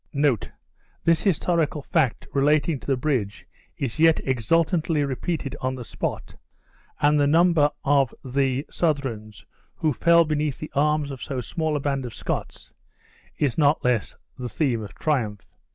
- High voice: No, medium, 145 Hz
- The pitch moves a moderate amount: Yes, average, 3.3 semitones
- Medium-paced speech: Yes, average, 150 wpm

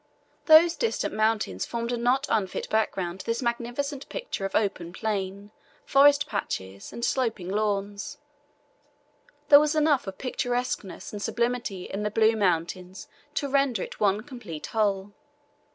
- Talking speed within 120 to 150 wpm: Yes, average, 140 wpm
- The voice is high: Yes, high, 220 Hz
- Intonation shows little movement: No, average, 4.7 semitones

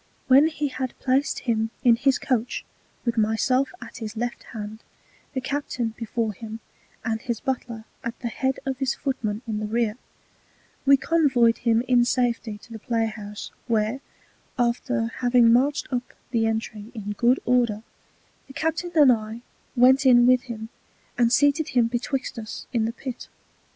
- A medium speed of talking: Yes, average, 165 wpm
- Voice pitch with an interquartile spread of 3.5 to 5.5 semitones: No, average, 2.7 semitones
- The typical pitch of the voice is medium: No, high, 240 Hz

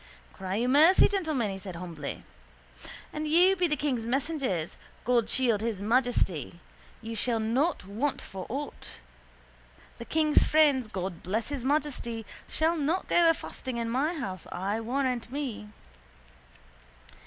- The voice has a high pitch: Yes, high, 245 Hz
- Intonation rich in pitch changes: Yes, wide, 6.0 semitones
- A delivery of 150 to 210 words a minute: No, average, 140 wpm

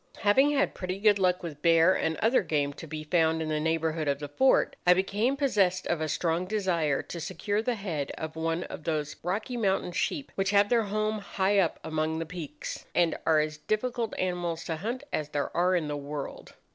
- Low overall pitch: No, medium, 175 Hz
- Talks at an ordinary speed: No, fast, 210 wpm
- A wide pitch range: No, average, 4.5 semitones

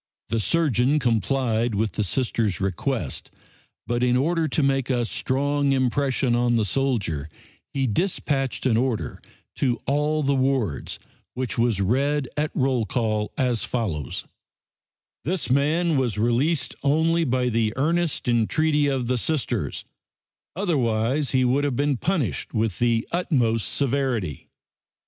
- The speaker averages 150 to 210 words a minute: No, slow, 135 wpm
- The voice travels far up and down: No, average, 3.8 semitones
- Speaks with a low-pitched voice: Yes, low, 130 Hz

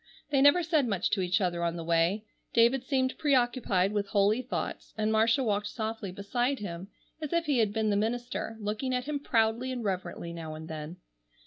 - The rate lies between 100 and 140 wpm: No, average, 200 wpm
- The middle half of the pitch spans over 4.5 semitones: Yes, average, 5.2 semitones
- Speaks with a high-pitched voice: Yes, high, 220 Hz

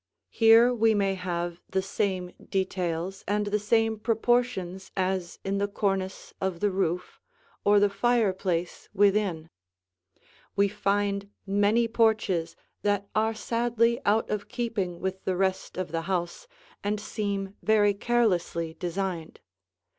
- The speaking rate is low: Yes, slow, 130 wpm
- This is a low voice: No, high, 200 Hz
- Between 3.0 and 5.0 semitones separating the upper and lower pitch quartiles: No, narrow, 2.5 semitones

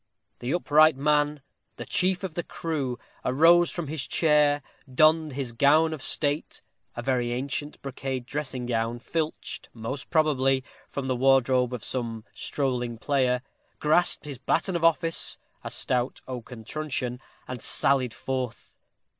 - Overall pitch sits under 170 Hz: Yes, low, 135 Hz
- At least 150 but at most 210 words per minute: No, average, 140 wpm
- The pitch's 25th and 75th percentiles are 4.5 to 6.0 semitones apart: No, average, 3.6 semitones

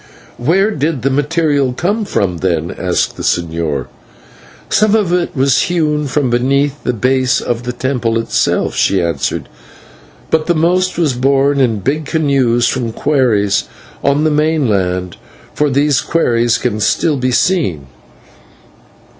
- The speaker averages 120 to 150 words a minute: Yes, average, 140 wpm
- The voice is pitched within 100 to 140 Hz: Yes, low, 135 Hz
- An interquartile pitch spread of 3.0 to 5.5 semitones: Yes, average, 5.1 semitones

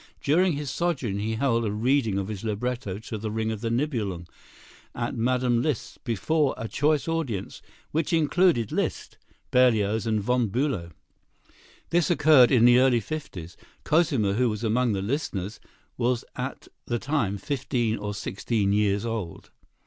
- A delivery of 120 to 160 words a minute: Yes, average, 155 wpm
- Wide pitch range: No, average, 4.9 semitones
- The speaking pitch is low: Yes, low, 115 Hz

